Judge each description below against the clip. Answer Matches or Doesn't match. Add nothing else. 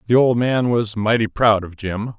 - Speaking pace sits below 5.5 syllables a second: Matches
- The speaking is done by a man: Matches